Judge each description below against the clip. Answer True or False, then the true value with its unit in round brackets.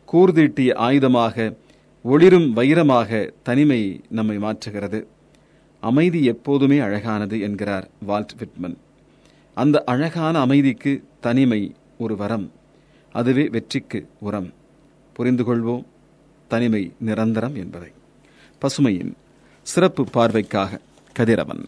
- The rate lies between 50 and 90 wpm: True (85 wpm)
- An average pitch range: True (4.9 semitones)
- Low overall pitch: True (120 Hz)